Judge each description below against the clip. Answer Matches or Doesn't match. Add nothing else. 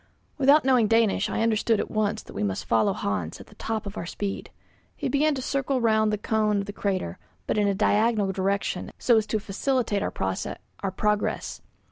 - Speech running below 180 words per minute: Doesn't match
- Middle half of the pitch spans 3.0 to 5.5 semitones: Doesn't match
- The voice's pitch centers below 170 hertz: Doesn't match